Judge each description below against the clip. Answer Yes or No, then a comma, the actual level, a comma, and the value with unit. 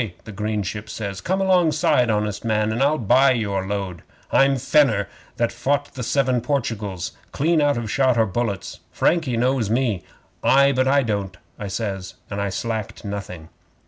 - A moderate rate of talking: Yes, average, 170 wpm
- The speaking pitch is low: Yes, low, 115 Hz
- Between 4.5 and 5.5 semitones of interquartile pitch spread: Yes, average, 5.0 semitones